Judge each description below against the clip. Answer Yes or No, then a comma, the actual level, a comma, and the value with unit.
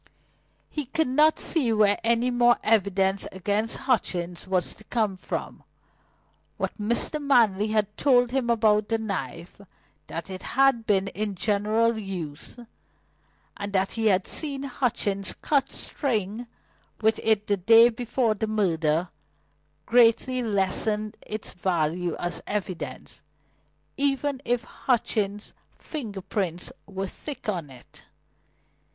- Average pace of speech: No, slow, 125 wpm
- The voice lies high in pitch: Yes, high, 215 Hz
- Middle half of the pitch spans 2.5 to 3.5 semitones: No, average, 3.9 semitones